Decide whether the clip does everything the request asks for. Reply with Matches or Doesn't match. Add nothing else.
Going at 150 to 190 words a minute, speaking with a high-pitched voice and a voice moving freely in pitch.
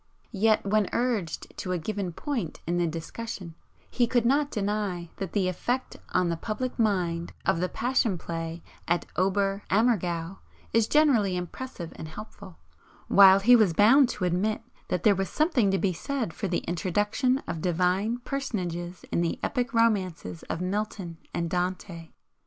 Doesn't match